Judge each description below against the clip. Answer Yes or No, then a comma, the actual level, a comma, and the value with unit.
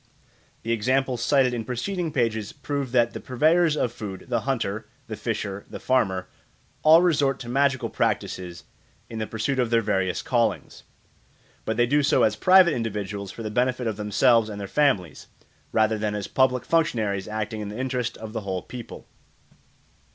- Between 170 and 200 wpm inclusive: Yes, average, 175 wpm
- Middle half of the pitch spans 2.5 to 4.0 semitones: Yes, average, 3.7 semitones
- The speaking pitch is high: No, low, 115 Hz